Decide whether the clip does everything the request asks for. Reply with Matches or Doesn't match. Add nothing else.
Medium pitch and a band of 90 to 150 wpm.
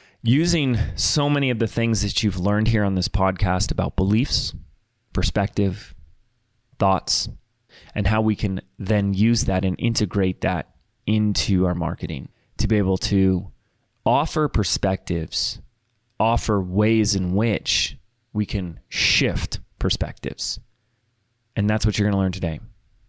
Doesn't match